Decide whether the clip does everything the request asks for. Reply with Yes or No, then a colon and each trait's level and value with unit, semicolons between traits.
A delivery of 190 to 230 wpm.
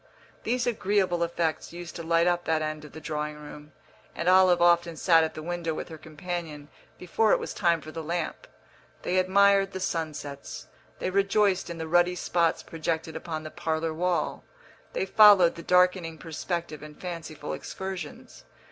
No: average, 170 wpm